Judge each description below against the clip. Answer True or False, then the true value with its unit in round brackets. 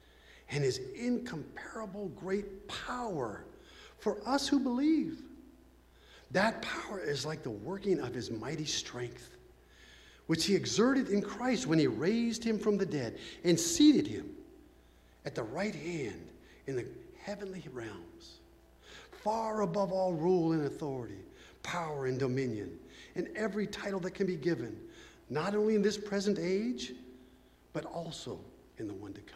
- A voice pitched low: False (195 Hz)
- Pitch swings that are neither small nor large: False (7.5 semitones)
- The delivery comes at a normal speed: True (145 wpm)